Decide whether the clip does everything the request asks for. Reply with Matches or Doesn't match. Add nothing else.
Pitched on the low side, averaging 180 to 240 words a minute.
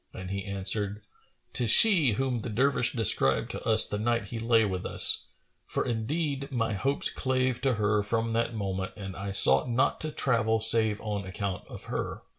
Matches